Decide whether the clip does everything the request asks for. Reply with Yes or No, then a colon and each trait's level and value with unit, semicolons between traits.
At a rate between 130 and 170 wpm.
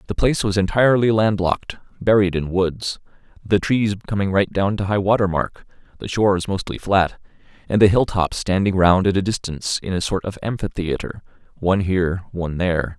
No: average, 180 wpm